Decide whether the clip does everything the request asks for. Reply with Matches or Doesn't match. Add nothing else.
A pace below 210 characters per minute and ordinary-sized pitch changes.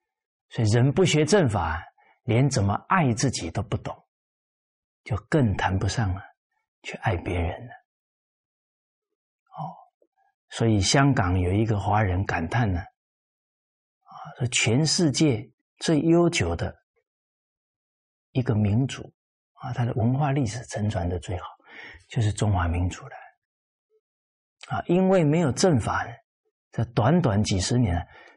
Doesn't match